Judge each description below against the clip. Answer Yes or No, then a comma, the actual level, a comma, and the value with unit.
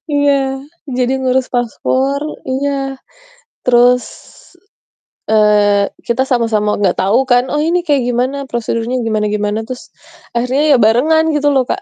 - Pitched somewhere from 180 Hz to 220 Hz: No, very high, 250 Hz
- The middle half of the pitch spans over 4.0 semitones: No, average, 3.5 semitones